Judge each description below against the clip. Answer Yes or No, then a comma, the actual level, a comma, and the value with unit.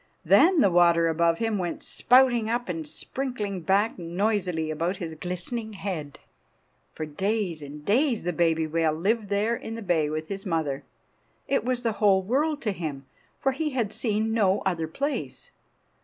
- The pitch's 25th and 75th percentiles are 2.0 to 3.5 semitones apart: No, wide, 5.4 semitones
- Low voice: No, high, 195 Hz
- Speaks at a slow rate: No, average, 170 wpm